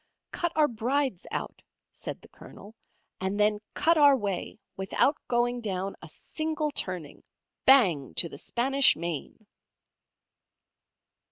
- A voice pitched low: No, high, 225 Hz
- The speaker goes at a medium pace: No, slow, 120 wpm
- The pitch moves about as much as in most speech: No, wide, 6.6 semitones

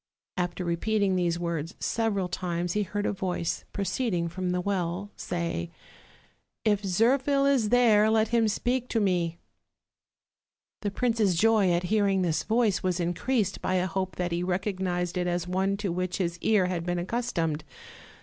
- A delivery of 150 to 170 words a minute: Yes, average, 165 wpm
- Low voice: No, medium, 185 Hz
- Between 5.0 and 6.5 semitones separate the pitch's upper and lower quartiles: No, average, 3.4 semitones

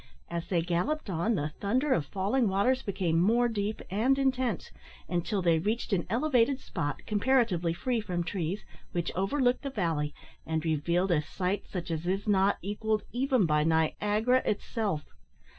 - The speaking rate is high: No, average, 160 wpm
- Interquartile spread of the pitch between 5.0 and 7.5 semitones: Yes, wide, 5.6 semitones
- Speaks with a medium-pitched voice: No, high, 200 Hz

